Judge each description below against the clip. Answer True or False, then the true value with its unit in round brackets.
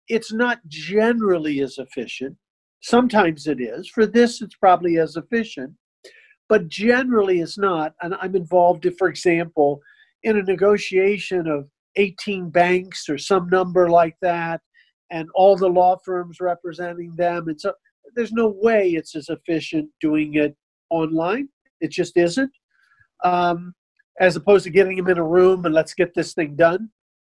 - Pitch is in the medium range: True (180 Hz)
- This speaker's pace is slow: False (155 wpm)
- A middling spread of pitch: True (3.4 semitones)